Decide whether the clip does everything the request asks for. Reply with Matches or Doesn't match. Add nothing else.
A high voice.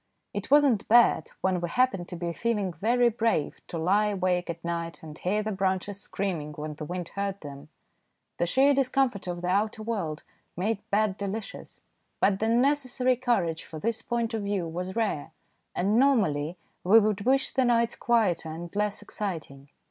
Matches